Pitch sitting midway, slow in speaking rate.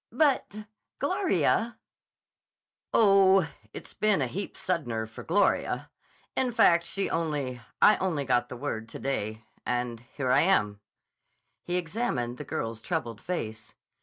Yes: medium, 155 Hz; slow, 130 wpm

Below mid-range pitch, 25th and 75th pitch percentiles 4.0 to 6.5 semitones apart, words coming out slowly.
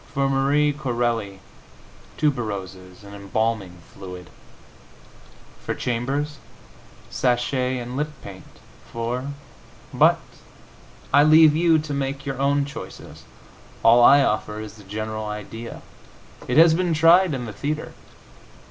Yes: low, 125 Hz; average, 5.0 semitones; slow, 120 wpm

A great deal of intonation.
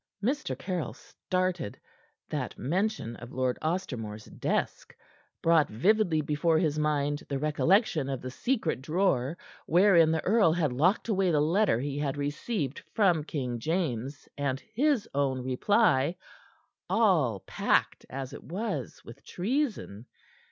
Yes: wide, 5.8 semitones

